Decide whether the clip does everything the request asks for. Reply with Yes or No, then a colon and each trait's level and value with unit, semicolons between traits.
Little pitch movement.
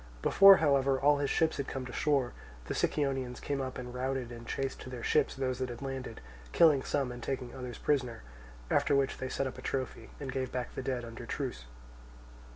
Yes: narrow, 1.7 semitones